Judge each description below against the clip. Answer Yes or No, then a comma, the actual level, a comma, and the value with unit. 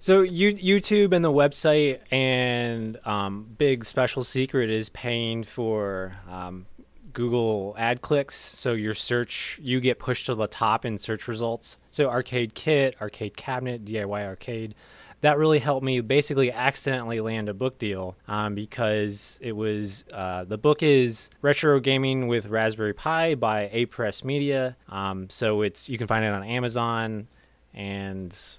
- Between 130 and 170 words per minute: Yes, average, 155 wpm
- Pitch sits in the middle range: No, low, 120 Hz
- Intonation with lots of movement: No, average, 4.0 semitones